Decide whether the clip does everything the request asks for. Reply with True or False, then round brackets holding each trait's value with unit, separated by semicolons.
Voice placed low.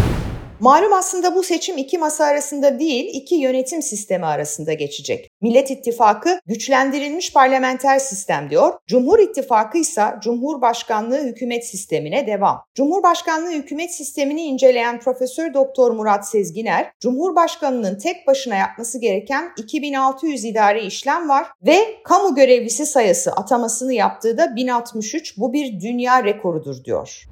False (265 Hz)